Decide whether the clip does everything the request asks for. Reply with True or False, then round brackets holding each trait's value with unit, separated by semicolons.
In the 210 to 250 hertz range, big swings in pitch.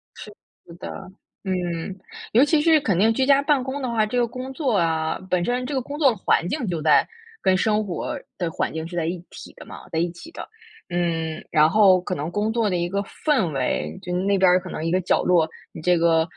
False (185 Hz; 6.2 semitones)